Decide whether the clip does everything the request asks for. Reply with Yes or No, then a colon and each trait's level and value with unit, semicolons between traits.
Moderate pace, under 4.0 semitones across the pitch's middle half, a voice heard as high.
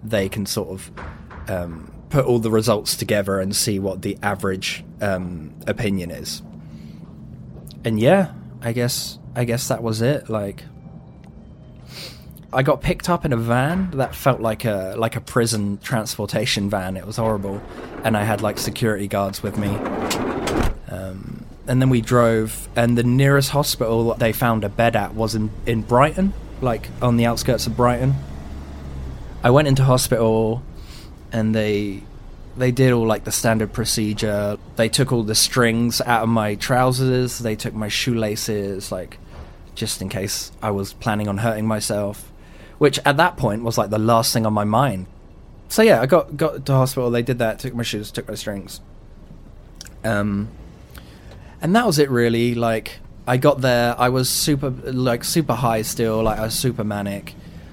No: average, 175 wpm; average, 3.4 semitones; low, 110 Hz